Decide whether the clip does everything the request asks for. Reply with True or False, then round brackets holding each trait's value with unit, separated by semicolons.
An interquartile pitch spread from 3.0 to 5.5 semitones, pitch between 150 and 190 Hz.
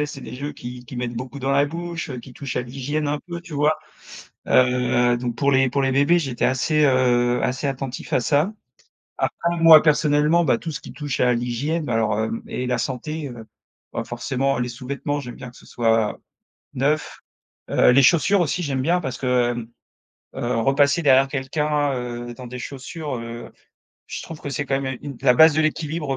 False (3.3 semitones; 135 Hz)